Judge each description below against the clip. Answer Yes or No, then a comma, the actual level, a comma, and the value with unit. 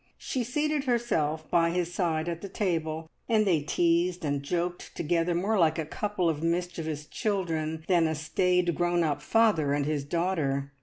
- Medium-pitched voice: Yes, medium, 170 Hz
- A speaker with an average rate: Yes, average, 170 wpm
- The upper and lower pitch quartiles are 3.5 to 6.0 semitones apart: No, narrow, 2.6 semitones